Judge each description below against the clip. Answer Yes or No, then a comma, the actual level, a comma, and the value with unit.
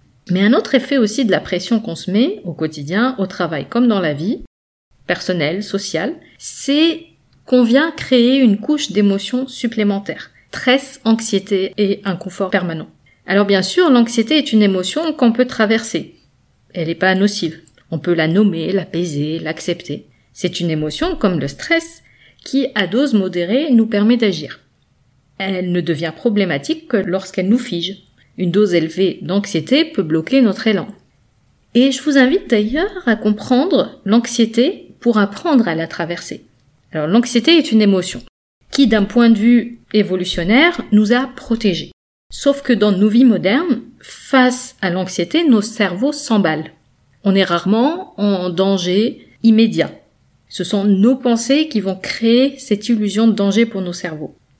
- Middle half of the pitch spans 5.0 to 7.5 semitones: Yes, wide, 5.4 semitones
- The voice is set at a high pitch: Yes, high, 210 Hz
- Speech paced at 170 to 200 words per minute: No, average, 155 wpm